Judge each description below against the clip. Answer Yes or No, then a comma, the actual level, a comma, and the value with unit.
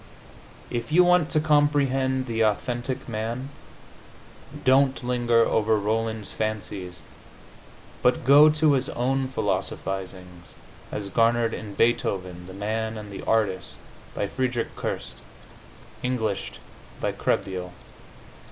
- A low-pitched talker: Yes, low, 115 Hz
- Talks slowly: Yes, slow, 110 wpm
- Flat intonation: No, average, 4.3 semitones